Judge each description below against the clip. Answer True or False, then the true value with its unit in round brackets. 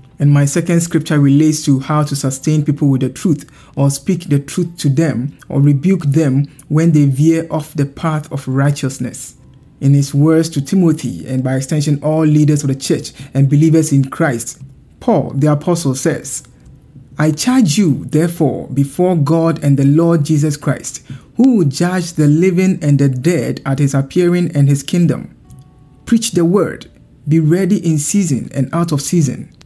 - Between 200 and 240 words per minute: False (175 wpm)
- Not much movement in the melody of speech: False (3.0 semitones)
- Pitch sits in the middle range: True (150 Hz)